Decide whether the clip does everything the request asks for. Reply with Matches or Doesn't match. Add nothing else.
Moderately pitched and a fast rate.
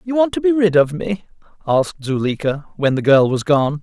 Matches